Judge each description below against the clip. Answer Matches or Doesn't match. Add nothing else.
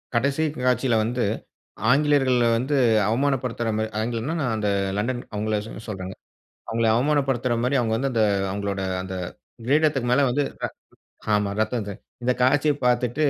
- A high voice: Doesn't match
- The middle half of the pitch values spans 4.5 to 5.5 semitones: Doesn't match